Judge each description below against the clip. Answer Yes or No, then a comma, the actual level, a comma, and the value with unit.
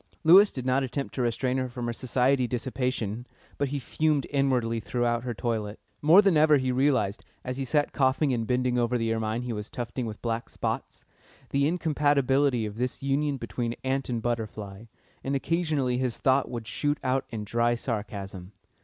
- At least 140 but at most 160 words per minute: No, average, 180 wpm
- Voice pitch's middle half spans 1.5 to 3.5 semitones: Yes, average, 3.0 semitones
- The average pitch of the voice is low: Yes, low, 125 Hz